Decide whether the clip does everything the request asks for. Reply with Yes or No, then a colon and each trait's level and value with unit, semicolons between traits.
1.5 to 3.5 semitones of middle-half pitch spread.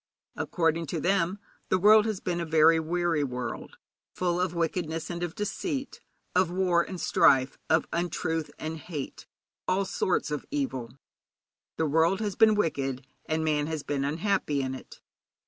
Yes: average, 3.2 semitones